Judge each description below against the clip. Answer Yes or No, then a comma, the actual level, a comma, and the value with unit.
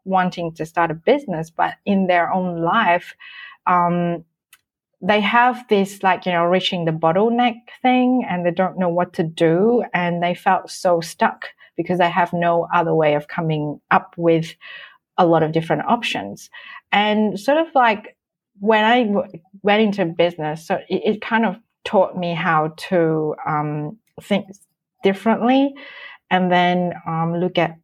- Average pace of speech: Yes, average, 160 wpm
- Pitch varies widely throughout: No, average, 3.9 semitones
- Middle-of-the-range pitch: Yes, medium, 180 Hz